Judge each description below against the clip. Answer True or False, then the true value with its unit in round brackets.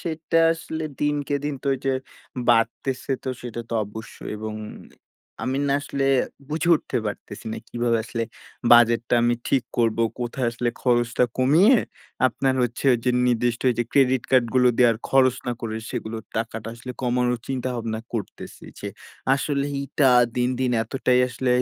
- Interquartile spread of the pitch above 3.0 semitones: False (2.6 semitones)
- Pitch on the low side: True (125 Hz)